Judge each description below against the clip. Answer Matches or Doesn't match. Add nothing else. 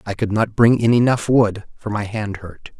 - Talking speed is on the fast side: Matches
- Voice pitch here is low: Matches